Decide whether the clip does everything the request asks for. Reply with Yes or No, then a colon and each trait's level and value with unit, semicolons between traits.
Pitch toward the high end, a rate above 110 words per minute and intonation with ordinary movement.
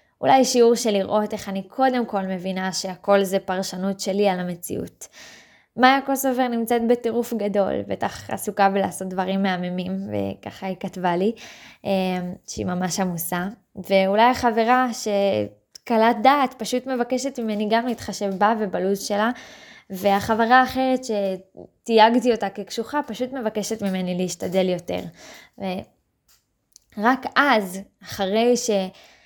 Yes: high, 205 Hz; average, 120 wpm; average, 3.8 semitones